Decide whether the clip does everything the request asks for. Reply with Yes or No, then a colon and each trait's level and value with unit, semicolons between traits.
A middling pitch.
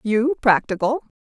No: high, 230 Hz